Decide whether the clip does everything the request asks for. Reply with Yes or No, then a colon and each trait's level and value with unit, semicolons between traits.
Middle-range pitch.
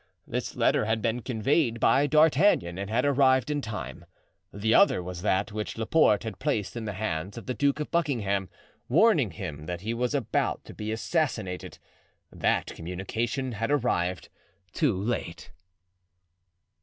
No: low, 110 Hz